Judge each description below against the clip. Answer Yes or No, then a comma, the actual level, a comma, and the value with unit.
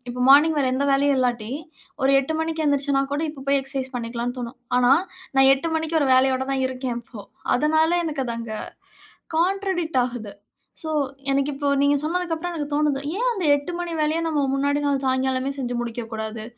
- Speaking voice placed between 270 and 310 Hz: Yes, very high, 275 Hz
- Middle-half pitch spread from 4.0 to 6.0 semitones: No, average, 3.6 semitones